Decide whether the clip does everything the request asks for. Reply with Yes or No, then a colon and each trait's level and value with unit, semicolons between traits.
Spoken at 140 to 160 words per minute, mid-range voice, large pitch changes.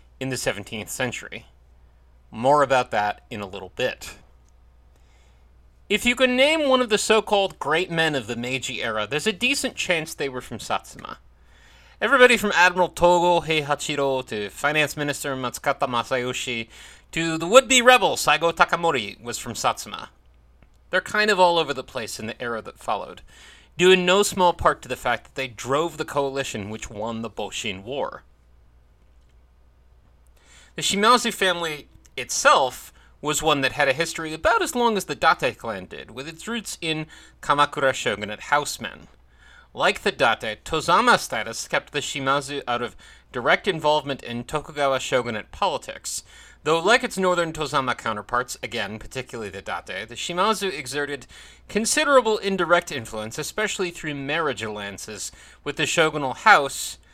Yes: average, 155 wpm; medium, 145 Hz; wide, 8.2 semitones